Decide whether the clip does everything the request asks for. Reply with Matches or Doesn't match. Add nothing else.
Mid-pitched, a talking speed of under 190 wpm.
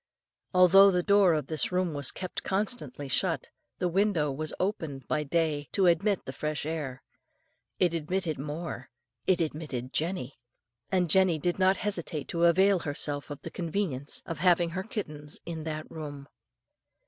Matches